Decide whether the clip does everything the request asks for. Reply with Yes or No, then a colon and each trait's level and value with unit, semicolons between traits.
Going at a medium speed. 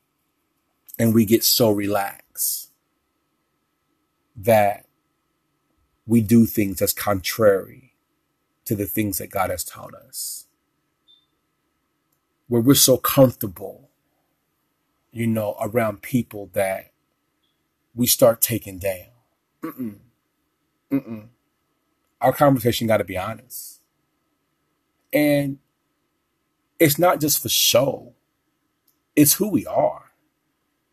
No: slow, 95 wpm